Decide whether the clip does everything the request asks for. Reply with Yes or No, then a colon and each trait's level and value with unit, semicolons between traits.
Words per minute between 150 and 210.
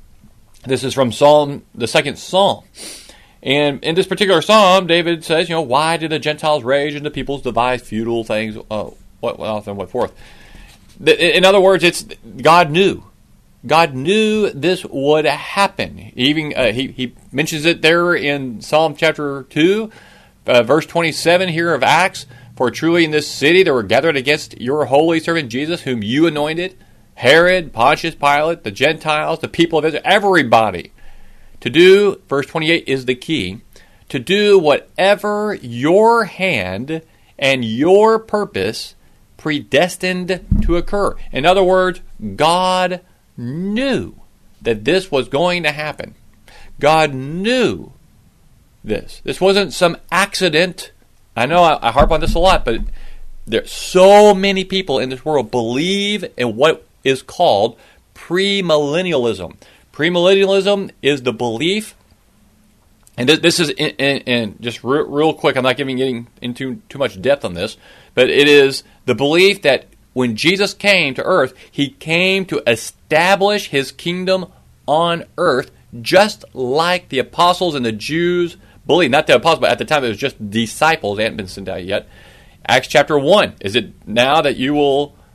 Yes: average, 160 wpm